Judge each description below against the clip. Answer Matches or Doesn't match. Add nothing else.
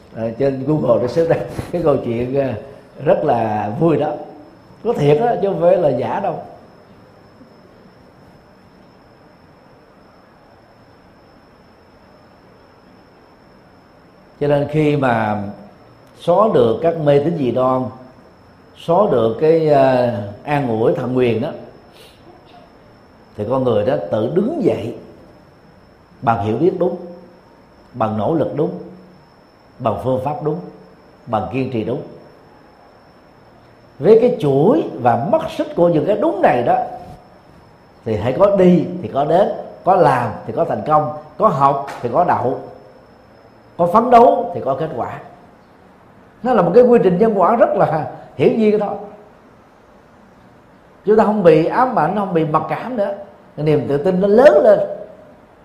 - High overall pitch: Doesn't match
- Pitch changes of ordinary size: Doesn't match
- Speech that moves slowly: Matches